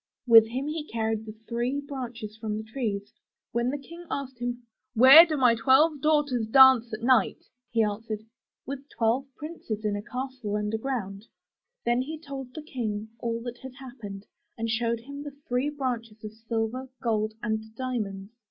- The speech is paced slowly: No, average, 170 wpm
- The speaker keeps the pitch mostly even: No, average, 3.3 semitones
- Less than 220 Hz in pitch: No, high, 240 Hz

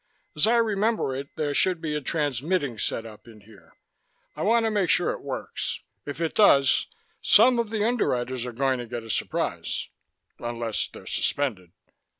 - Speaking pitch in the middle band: Yes, medium, 145 Hz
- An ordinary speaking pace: Yes, average, 170 wpm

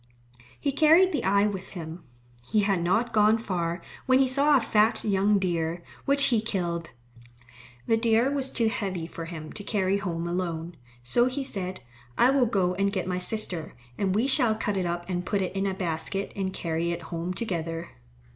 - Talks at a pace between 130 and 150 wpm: No, average, 195 wpm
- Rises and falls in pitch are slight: No, average, 4.6 semitones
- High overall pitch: Yes, high, 195 Hz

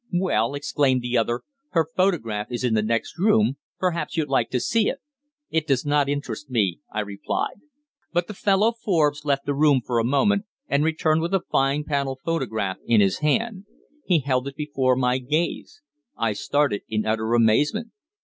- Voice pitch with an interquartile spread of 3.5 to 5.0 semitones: No, wide, 5.6 semitones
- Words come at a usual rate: Yes, average, 180 wpm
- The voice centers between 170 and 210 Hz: No, medium, 140 Hz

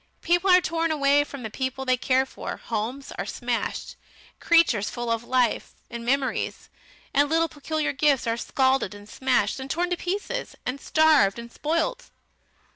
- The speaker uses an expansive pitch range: No, average, 5.0 semitones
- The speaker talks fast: No, average, 165 wpm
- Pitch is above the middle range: Yes, very high, 275 Hz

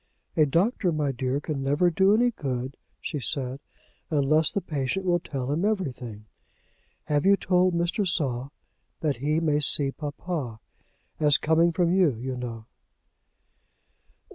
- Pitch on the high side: No, medium, 150 Hz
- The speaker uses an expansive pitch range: No, average, 4.4 semitones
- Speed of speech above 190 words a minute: No, average, 140 wpm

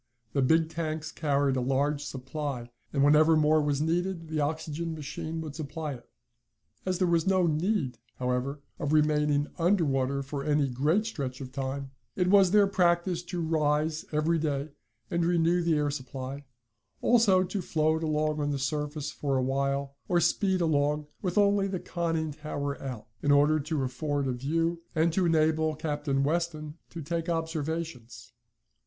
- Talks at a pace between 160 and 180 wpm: Yes, average, 165 wpm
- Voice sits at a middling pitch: Yes, medium, 155 Hz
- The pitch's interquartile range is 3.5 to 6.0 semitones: No, average, 2.9 semitones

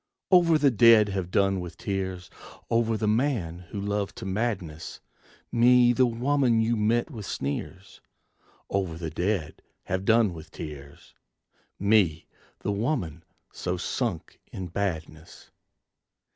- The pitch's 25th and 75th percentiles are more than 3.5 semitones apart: Yes, average, 4.6 semitones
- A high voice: No, low, 100 Hz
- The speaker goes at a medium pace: No, slow, 130 wpm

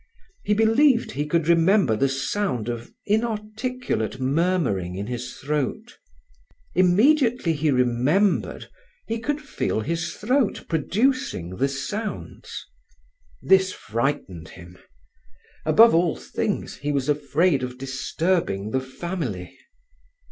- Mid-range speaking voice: Yes, medium, 160 Hz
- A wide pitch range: Yes, wide, 8.6 semitones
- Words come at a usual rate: No, slow, 110 wpm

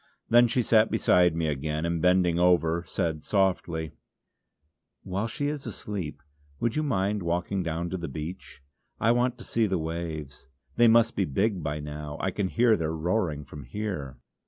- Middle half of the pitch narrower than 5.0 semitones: No, wide, 5.4 semitones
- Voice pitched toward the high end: No, very low, 90 Hz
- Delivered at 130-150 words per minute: No, average, 175 wpm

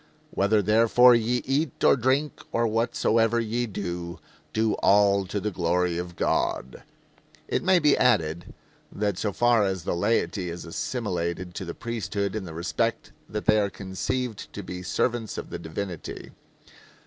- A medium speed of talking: Yes, average, 160 wpm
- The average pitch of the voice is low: Yes, low, 105 Hz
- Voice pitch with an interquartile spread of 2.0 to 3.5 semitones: No, average, 4.6 semitones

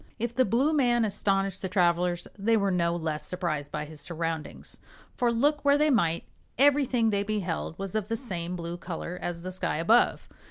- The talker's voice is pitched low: No, high, 195 Hz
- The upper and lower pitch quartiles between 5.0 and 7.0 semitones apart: Yes, wide, 5.5 semitones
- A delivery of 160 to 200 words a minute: Yes, average, 190 wpm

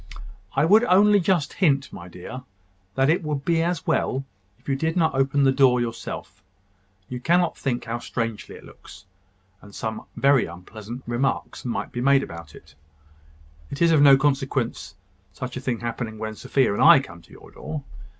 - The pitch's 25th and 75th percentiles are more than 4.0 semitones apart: Yes, average, 4.5 semitones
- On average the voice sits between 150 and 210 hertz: No, low, 135 Hz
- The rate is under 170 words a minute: No, average, 180 wpm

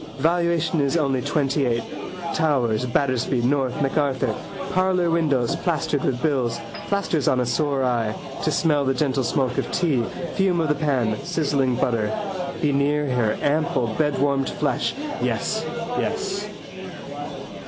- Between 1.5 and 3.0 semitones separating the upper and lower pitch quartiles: No, average, 3.7 semitones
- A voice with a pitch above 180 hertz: No, medium, 140 Hz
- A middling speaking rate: No, slow, 130 wpm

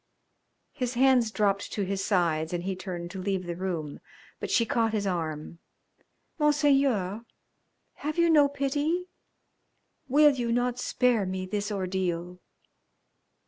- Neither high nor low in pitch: No, high, 205 Hz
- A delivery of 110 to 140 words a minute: Yes, slow, 135 wpm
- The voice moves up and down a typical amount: No, wide, 6.5 semitones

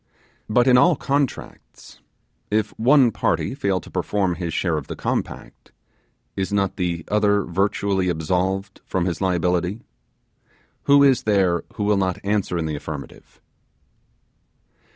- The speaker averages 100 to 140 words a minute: Yes, slow, 135 wpm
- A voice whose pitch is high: No, very low, 95 Hz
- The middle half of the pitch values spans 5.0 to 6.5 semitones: No, average, 3.1 semitones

